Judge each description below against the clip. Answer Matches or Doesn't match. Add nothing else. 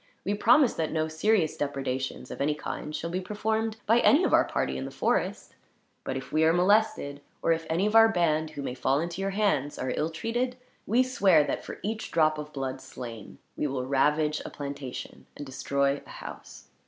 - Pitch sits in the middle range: Matches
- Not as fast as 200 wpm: Doesn't match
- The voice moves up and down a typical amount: Doesn't match